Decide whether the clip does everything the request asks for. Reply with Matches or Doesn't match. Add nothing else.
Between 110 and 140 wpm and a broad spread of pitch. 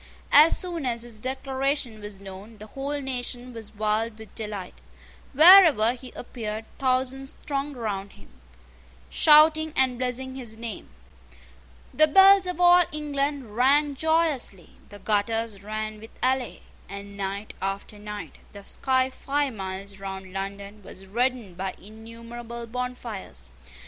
Doesn't match